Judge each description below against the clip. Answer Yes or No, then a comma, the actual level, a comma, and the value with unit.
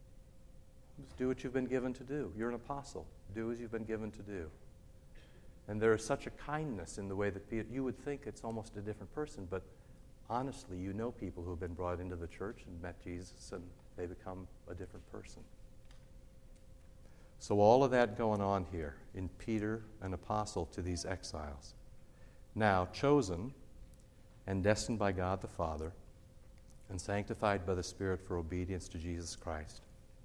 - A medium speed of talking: Yes, average, 175 wpm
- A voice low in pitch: Yes, low, 100 Hz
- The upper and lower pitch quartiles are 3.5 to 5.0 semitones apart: Yes, average, 4.2 semitones